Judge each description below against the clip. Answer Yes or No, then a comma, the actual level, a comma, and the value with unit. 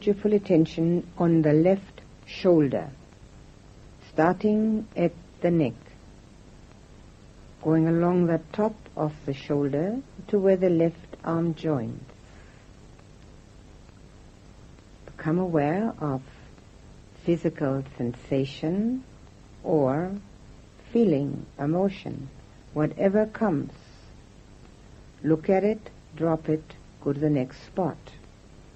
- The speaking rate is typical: No, slow, 90 wpm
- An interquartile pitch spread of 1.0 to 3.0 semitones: No, average, 4.6 semitones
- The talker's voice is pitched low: No, medium, 165 Hz